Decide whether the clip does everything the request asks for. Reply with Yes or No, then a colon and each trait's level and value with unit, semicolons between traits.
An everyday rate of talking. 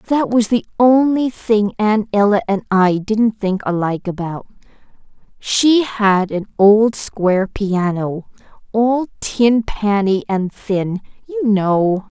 No: slow, 130 wpm